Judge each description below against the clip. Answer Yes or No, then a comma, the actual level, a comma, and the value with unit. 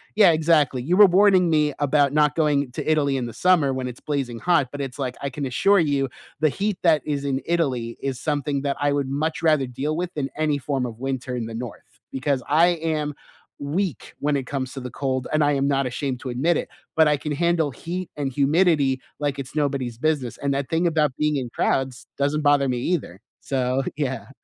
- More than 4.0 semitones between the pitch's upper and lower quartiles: No, average, 2.8 semitones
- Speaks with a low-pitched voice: No, medium, 145 Hz